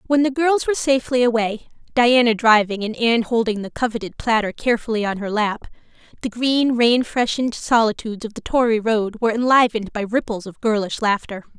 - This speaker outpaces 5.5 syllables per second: Yes, 6.0 syllables/s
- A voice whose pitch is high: Yes, high, 230 Hz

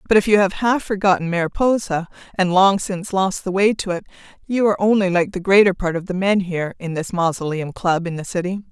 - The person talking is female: Yes, female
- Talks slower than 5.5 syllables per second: No, 6.0 syllables/s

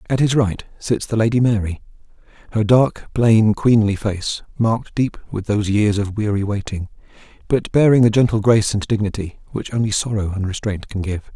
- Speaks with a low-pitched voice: Yes, low, 105 Hz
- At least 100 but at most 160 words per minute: No, average, 180 wpm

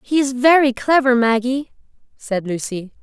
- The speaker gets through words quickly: No, average, 140 wpm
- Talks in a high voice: Yes, very high, 250 Hz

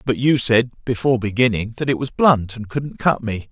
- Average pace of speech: No, fast, 220 wpm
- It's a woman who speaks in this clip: No, male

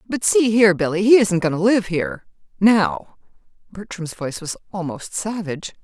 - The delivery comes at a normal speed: Yes, average, 155 wpm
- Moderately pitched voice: No, high, 195 Hz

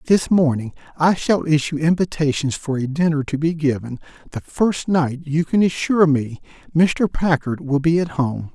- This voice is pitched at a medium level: Yes, medium, 155 Hz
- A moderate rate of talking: Yes, average, 175 wpm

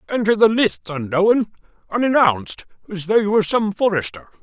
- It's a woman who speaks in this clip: No, male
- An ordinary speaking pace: Yes, average, 150 wpm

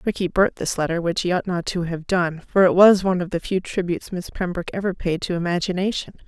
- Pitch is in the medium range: Yes, medium, 180 Hz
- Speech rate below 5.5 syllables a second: No, 6.1 syllables/s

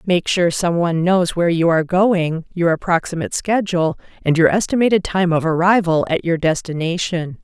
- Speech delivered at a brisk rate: No, average, 160 wpm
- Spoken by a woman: Yes, female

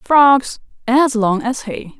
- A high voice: Yes, high, 245 Hz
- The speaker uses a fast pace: No, average, 150 wpm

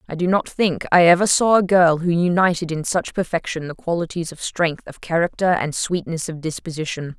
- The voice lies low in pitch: No, medium, 170 Hz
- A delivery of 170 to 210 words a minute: Yes, average, 200 wpm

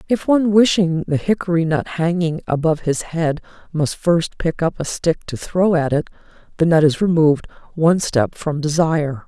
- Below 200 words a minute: Yes, average, 180 wpm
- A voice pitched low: No, medium, 165 Hz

